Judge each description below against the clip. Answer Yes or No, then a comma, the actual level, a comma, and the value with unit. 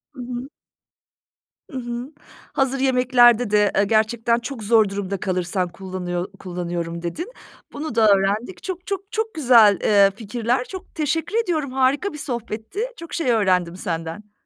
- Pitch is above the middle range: Yes, high, 230 Hz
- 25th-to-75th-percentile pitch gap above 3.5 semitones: Yes, wide, 5.4 semitones